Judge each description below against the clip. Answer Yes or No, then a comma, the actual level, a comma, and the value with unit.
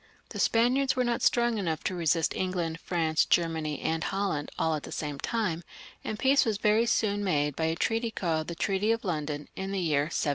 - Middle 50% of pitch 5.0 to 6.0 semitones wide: Yes, wide, 5.6 semitones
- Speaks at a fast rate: Yes, fast, 210 wpm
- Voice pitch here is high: No, medium, 180 Hz